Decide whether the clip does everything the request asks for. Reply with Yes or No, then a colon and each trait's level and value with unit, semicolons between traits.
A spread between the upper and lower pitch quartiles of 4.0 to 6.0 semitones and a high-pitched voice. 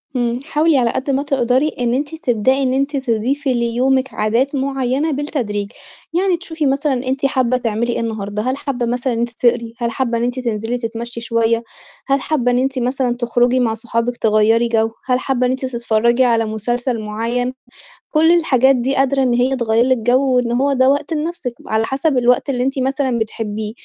No: narrow, 2.5 semitones; very high, 250 Hz